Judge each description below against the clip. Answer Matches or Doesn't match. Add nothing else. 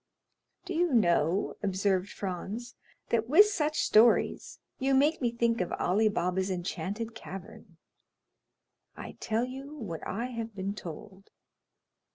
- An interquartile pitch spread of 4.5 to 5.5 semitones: Matches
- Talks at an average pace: Doesn't match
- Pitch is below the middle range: Doesn't match